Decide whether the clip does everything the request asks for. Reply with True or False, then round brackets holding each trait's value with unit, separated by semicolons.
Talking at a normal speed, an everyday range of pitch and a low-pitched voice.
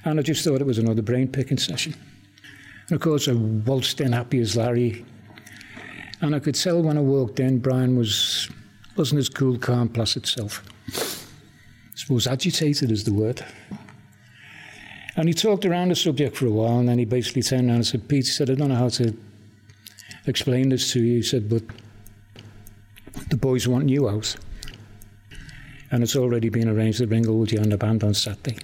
True (185 wpm; 3.9 semitones; 125 Hz)